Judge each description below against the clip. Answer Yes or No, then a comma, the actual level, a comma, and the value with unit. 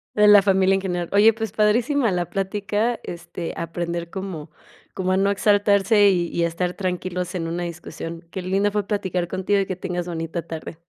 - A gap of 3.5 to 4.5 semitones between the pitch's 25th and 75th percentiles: No, average, 2.8 semitones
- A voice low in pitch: No, medium, 185 Hz